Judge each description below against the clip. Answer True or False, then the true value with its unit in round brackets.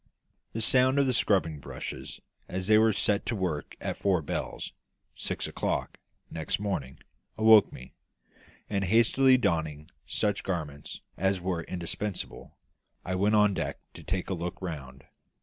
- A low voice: True (95 Hz)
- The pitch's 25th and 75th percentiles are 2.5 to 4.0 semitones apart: False (4.5 semitones)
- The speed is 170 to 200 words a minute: False (150 wpm)